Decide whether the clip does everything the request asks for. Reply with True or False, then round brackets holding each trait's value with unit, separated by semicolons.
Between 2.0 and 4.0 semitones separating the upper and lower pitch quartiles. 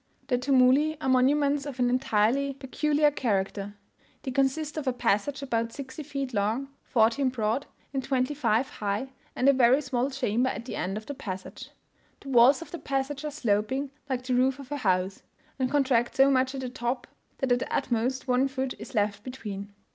True (2.9 semitones)